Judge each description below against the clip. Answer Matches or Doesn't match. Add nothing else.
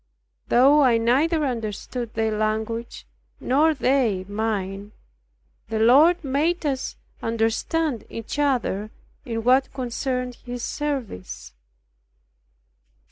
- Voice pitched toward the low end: Doesn't match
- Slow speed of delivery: Matches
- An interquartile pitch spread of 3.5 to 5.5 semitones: Matches